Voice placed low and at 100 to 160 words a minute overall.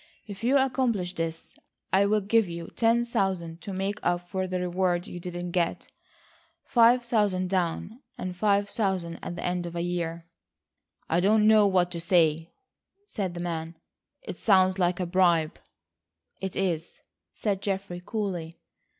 No: medium, 185 Hz; average, 155 wpm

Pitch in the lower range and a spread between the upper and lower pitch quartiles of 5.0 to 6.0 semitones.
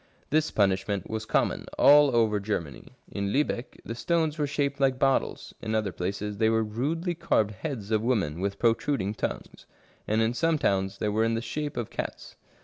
Yes: low, 110 Hz; wide, 5.4 semitones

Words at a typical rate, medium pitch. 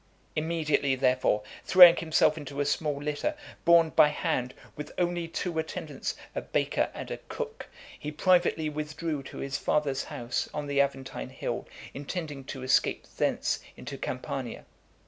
Yes: average, 145 wpm; medium, 150 Hz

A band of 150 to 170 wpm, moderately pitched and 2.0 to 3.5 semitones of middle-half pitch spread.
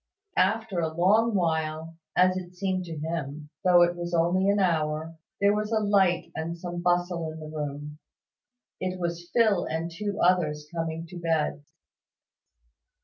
Yes: average, 155 wpm; medium, 175 Hz; narrow, 2.6 semitones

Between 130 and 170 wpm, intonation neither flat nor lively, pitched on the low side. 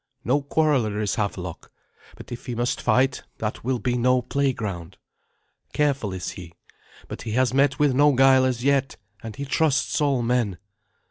Yes: average, 165 wpm; average, 3.9 semitones; low, 125 Hz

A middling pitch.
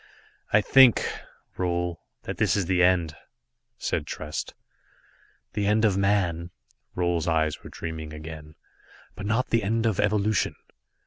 No: very low, 90 Hz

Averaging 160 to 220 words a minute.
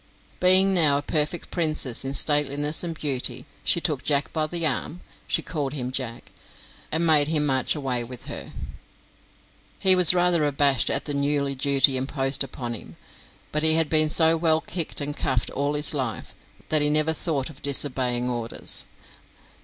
Yes: average, 170 wpm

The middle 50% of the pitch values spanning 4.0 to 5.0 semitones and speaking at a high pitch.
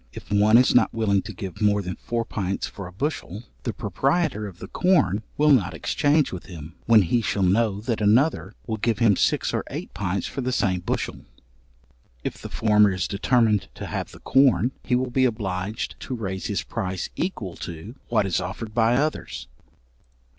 No: average, 4.3 semitones; low, 105 Hz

